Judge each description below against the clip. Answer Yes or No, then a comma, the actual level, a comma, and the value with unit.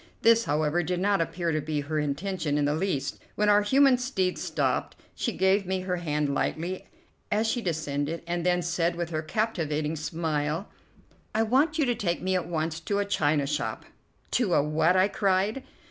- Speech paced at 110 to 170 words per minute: No, average, 190 wpm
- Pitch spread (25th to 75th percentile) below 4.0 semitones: No, average, 4.6 semitones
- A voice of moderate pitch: Yes, medium, 175 Hz